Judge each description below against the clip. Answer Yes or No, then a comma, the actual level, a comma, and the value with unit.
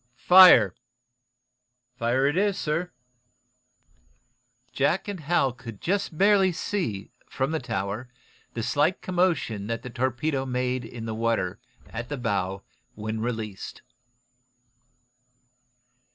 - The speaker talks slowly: Yes, slow, 110 wpm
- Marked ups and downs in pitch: Yes, wide, 6.6 semitones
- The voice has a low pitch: Yes, low, 125 Hz